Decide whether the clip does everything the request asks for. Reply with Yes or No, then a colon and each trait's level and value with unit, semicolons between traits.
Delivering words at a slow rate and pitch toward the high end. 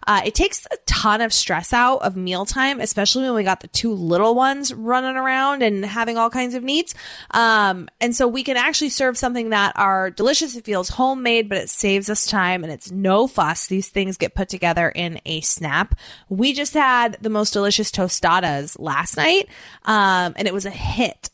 No: fast, 205 wpm; high, 215 Hz